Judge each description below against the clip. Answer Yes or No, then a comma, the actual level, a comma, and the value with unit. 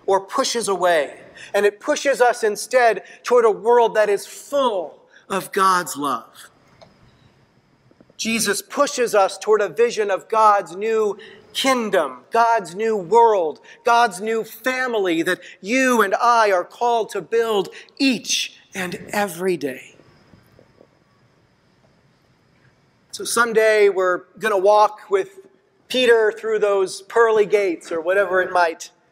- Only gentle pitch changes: No, average, 3.5 semitones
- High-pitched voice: Yes, high, 215 Hz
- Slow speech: Yes, slow, 125 wpm